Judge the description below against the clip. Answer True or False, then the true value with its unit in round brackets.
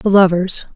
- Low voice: False (185 Hz)